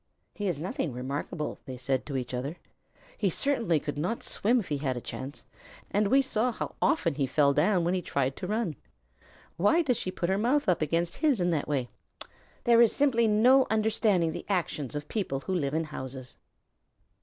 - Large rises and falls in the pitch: Yes, wide, 7.4 semitones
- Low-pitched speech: No, medium, 175 Hz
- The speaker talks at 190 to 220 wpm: Yes, average, 200 wpm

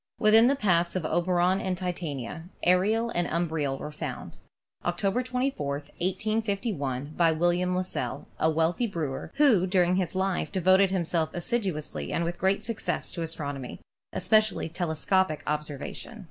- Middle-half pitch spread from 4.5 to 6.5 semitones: No, average, 3.6 semitones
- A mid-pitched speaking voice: Yes, medium, 175 Hz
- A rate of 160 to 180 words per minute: No, average, 145 wpm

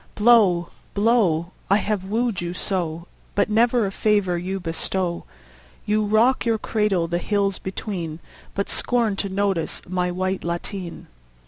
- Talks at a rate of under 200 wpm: Yes, average, 140 wpm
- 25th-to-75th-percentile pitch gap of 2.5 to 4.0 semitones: Yes, average, 3.3 semitones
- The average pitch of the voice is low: No, high, 195 Hz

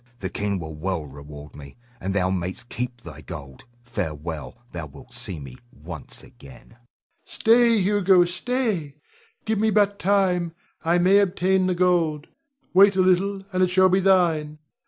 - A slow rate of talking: No, average, 160 wpm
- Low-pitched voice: No, medium, 170 Hz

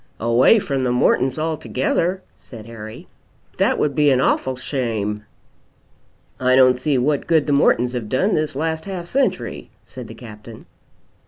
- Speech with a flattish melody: No, average, 4.5 semitones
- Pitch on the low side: Yes, low, 130 Hz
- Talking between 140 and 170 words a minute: Yes, average, 155 wpm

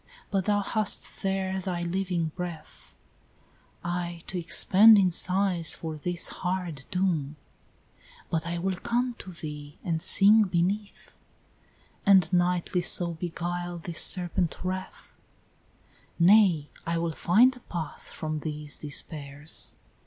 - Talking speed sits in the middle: No, slow, 130 wpm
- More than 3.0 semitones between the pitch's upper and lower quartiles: No, narrow, 2.6 semitones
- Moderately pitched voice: Yes, medium, 175 Hz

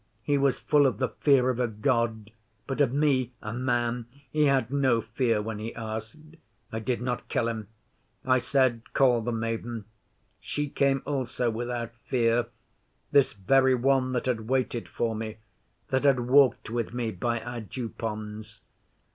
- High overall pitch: No, low, 120 Hz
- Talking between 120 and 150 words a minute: No, average, 165 wpm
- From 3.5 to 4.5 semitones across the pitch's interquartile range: No, average, 2.8 semitones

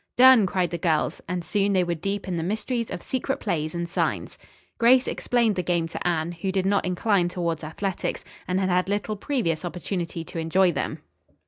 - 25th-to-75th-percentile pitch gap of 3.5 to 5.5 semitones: No, average, 3.0 semitones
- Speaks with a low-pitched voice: No, medium, 180 Hz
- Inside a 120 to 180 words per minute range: No, average, 200 wpm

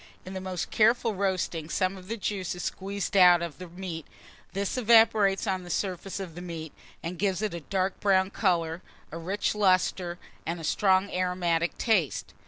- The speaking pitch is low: No, medium, 185 Hz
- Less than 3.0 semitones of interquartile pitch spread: Yes, narrow, 2.4 semitones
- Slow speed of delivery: No, average, 185 wpm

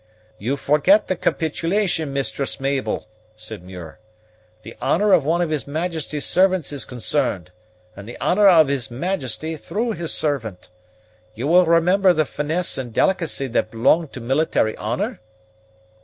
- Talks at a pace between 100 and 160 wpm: Yes, average, 145 wpm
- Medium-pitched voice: Yes, medium, 150 Hz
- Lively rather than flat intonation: Yes, wide, 6.1 semitones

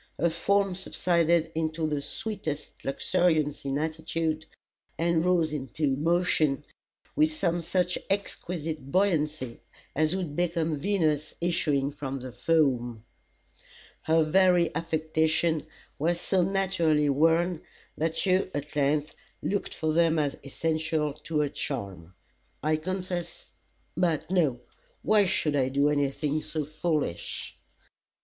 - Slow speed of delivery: Yes, slow, 120 wpm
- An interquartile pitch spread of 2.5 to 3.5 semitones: Yes, average, 2.9 semitones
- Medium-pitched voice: Yes, medium, 160 Hz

